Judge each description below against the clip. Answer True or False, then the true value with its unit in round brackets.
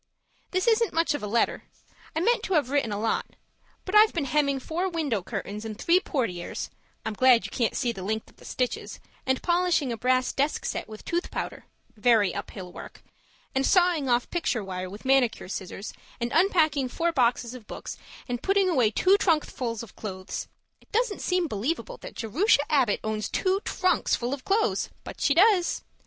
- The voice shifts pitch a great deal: True (7.6 semitones)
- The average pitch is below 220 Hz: False (265 Hz)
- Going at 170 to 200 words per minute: True (190 wpm)